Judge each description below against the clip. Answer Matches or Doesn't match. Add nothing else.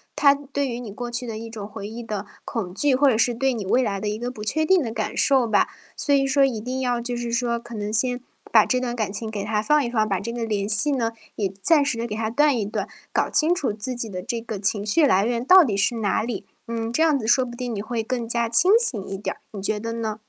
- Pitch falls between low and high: Doesn't match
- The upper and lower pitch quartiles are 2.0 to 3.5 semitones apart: Matches